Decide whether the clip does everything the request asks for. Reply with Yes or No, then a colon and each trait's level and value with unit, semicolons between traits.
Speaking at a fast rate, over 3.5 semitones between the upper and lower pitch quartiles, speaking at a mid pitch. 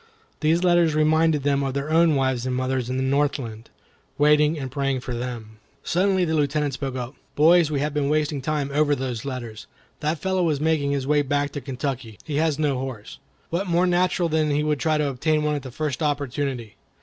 No: fast, 210 wpm; average, 2.8 semitones; medium, 145 Hz